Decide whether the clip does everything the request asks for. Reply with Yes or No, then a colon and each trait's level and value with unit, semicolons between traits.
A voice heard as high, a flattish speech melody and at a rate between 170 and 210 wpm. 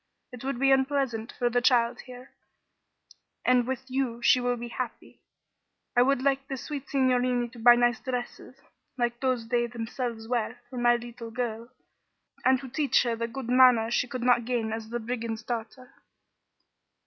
Yes: high, 245 Hz; narrow, 1.5 semitones; average, 175 wpm